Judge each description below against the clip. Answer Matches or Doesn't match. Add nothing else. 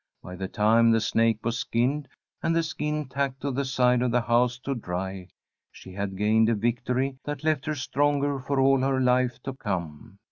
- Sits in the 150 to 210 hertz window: Doesn't match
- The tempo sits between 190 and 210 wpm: Matches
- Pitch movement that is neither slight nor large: Matches